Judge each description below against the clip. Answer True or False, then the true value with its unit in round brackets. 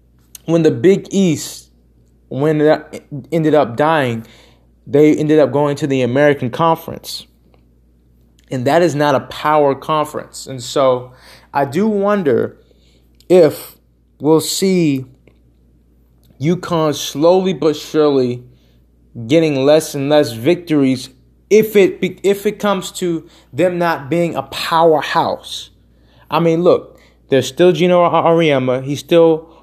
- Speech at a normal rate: False (125 wpm)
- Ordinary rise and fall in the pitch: False (6.1 semitones)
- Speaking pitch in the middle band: True (145 Hz)